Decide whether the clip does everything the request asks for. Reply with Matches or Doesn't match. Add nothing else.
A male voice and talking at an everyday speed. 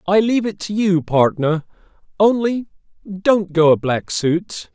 Matches